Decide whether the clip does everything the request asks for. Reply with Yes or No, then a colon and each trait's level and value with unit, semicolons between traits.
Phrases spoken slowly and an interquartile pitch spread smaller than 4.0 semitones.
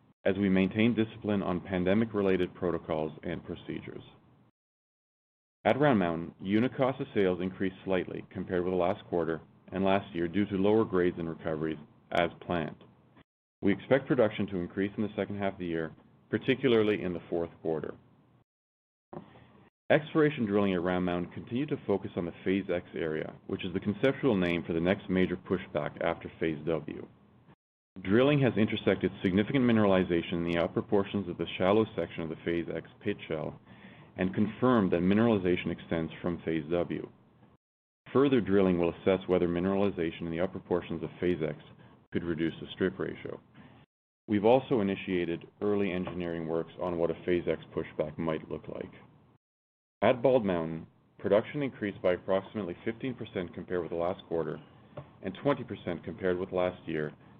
No: average, 165 wpm; average, 3.4 semitones